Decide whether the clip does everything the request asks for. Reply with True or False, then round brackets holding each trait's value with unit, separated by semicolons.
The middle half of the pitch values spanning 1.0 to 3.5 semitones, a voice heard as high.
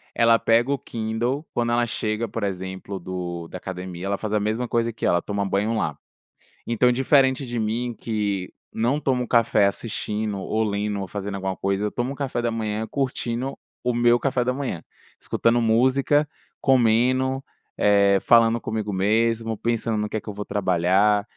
False (3.1 semitones; 110 Hz)